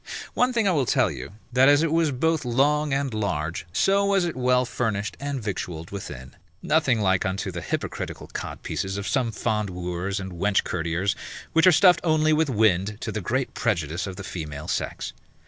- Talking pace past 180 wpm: Yes, average, 190 wpm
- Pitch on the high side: No, low, 110 Hz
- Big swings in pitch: Yes, wide, 7.7 semitones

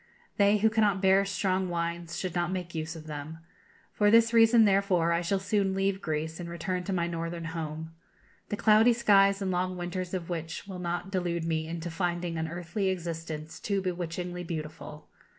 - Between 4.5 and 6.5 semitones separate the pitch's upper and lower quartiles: No, average, 2.8 semitones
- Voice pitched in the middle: Yes, medium, 175 Hz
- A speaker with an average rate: Yes, average, 185 wpm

